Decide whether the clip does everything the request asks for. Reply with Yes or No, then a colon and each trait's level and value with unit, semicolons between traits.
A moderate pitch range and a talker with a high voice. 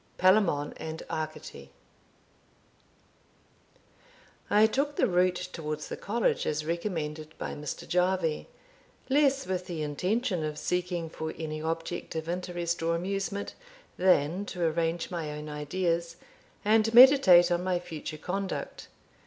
No: average, 3.0 semitones; medium, 175 Hz